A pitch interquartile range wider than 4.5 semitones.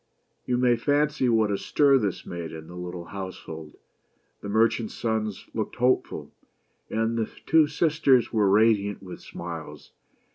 Yes: average, 5.2 semitones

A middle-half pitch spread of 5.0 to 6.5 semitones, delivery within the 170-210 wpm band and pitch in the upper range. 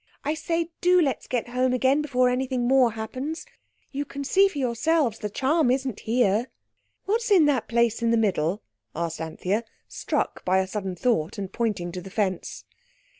Yes: average, 5.3 semitones; average, 175 wpm; high, 245 Hz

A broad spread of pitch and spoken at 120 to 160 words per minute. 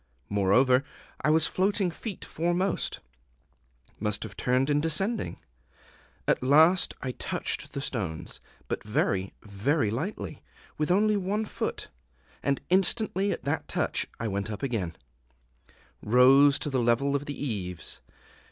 Yes: wide, 7.9 semitones; slow, 135 wpm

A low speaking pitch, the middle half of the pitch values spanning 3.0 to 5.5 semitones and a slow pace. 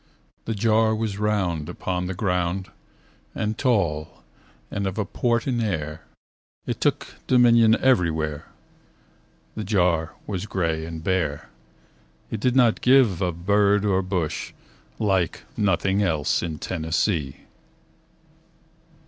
Yes: very low, 95 Hz; average, 4.5 semitones; slow, 120 wpm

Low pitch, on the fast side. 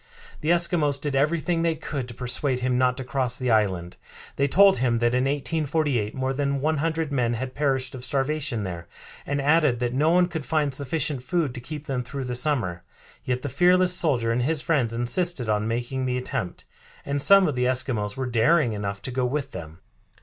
Yes: low, 130 Hz; fast, 210 wpm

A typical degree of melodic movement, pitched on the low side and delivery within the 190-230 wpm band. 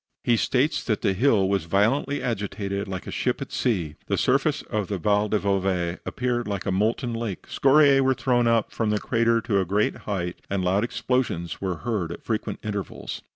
Yes: average, 3.7 semitones; low, 105 Hz; average, 200 wpm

